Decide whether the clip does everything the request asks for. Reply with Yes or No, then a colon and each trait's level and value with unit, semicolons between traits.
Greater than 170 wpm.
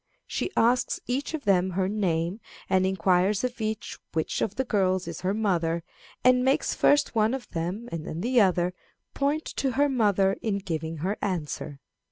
Yes: average, 180 wpm